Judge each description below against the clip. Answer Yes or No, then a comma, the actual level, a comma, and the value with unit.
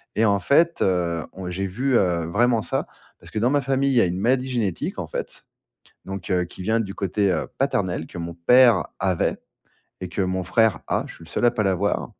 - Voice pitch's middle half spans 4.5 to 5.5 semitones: Yes, average, 5.1 semitones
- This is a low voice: Yes, low, 100 Hz